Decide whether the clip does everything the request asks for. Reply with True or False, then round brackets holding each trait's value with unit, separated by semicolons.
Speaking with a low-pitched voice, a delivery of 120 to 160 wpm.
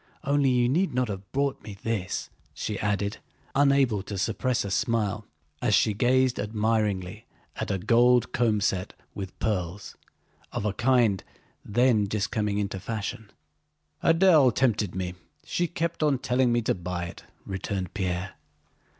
True (110 Hz; 150 wpm)